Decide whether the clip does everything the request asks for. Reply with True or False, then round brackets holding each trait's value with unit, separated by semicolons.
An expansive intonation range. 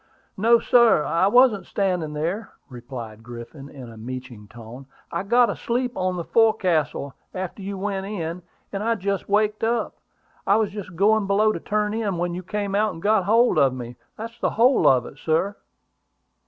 True (6.3 semitones)